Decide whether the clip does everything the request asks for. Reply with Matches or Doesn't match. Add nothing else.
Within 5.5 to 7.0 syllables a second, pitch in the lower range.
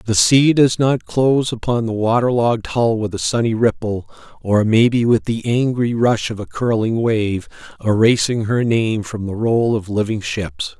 Doesn't match